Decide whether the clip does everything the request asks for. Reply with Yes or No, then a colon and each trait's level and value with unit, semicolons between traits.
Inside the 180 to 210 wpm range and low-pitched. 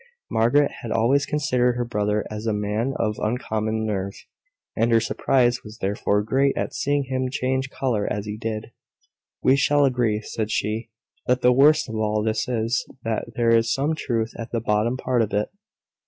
Yes: average, 185 wpm; low, 115 Hz